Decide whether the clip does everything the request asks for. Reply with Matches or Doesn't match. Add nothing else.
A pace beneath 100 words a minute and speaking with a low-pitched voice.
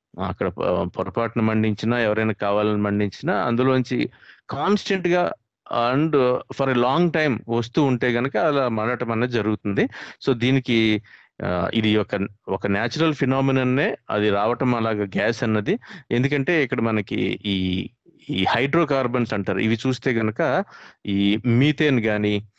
Doesn't match